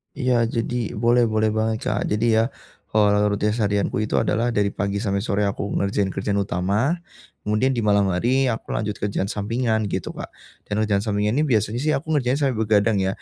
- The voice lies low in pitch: Yes, low, 105 Hz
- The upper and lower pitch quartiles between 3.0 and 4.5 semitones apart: No, narrow, 2.5 semitones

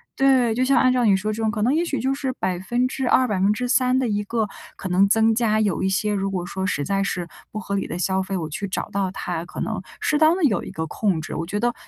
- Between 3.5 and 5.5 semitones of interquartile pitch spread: Yes, average, 4.6 semitones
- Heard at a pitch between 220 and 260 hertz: No, high, 210 Hz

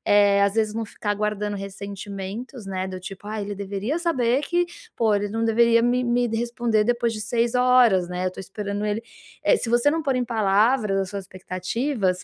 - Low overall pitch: No, high, 215 Hz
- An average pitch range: Yes, average, 3.2 semitones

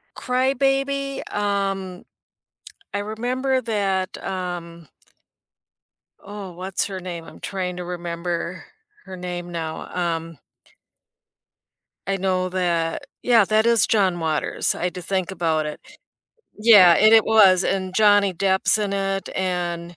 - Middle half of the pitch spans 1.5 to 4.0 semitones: Yes, average, 2.9 semitones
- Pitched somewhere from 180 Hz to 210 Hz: Yes, high, 190 Hz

